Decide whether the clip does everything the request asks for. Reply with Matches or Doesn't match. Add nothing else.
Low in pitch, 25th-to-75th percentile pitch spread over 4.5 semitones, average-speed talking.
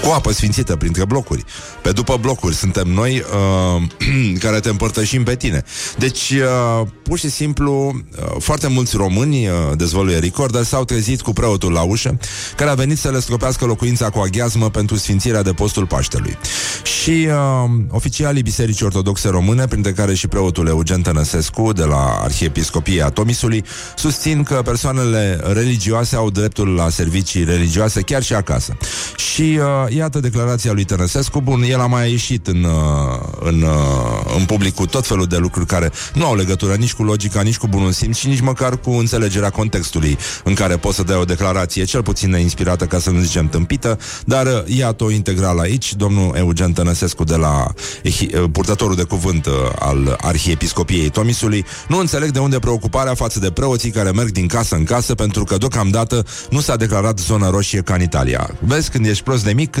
Doesn't match